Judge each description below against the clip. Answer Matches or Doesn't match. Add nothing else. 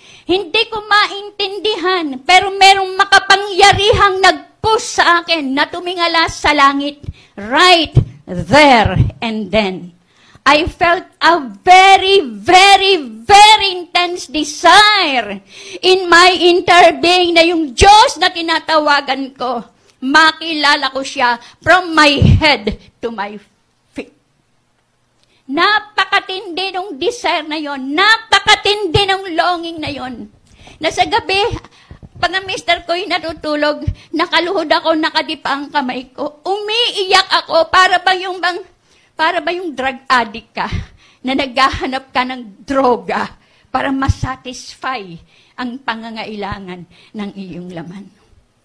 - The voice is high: Matches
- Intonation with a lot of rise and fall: Matches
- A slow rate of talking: Matches